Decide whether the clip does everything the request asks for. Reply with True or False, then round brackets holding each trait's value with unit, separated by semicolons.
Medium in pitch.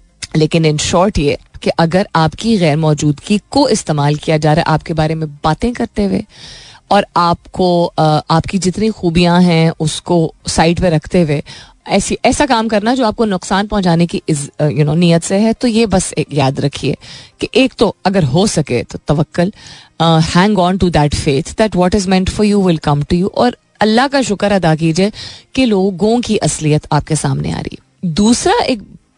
True (175 Hz)